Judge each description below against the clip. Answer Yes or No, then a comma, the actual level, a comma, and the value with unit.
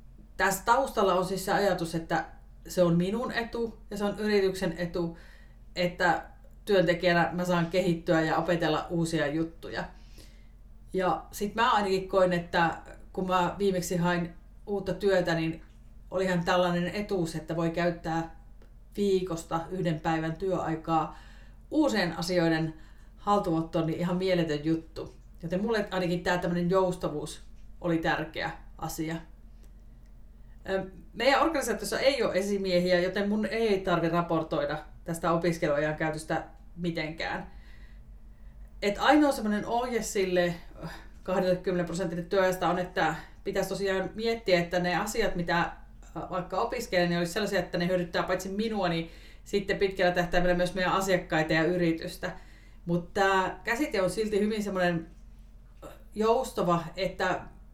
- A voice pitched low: No, medium, 180 Hz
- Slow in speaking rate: No, average, 125 wpm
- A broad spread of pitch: No, narrow, 2.6 semitones